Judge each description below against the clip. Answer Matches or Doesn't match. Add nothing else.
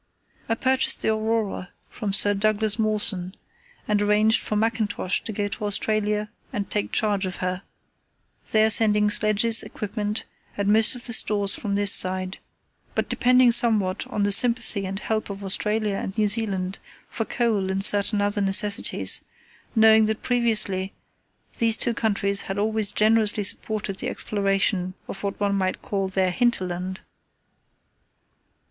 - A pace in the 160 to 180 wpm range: Doesn't match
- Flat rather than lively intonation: Matches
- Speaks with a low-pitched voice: Doesn't match